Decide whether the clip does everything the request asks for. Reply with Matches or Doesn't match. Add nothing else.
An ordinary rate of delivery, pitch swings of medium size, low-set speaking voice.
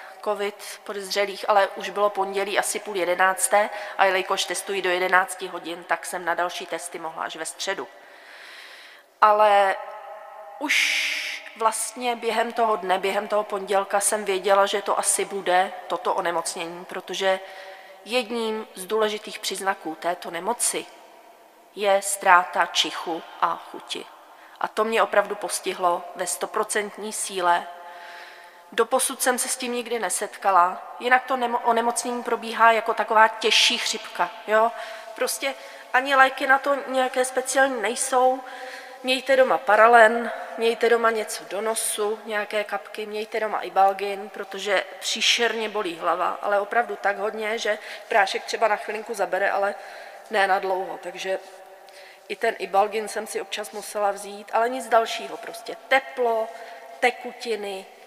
Doesn't match